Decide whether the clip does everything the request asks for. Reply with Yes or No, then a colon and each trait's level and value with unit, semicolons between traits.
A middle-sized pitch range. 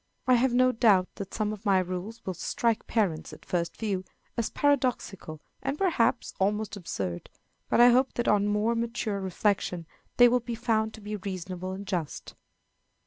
Yes: average, 3.9 semitones